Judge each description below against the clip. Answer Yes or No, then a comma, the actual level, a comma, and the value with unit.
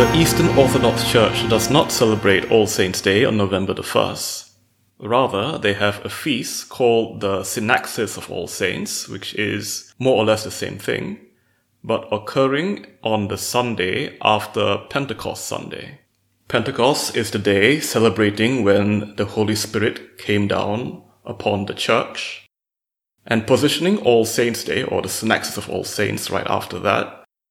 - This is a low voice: Yes, low, 110 Hz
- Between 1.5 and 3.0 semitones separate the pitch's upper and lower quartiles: Yes, narrow, 2.6 semitones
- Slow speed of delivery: No, average, 150 wpm